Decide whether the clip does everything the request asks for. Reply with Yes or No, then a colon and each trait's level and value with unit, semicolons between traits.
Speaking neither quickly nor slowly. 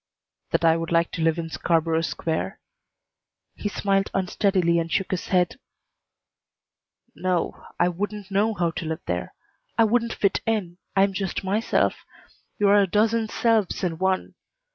Yes: average, 160 wpm